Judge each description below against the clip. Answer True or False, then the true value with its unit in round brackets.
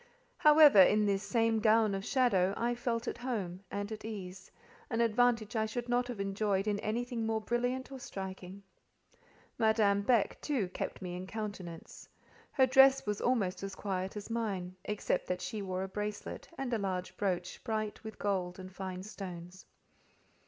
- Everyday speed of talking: True (170 wpm)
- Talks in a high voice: True (210 Hz)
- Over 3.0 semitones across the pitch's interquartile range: True (3.5 semitones)